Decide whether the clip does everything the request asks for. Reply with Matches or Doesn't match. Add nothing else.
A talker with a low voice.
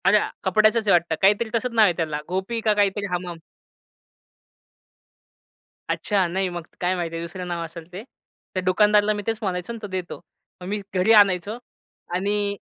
Doesn't match